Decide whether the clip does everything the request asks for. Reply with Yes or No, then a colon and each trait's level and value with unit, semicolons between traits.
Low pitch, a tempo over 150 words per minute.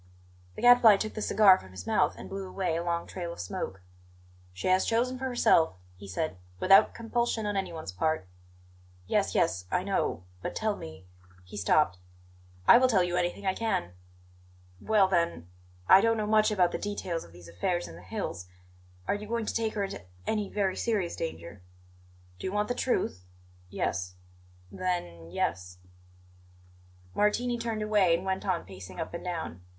No: medium, 185 Hz; average, 180 wpm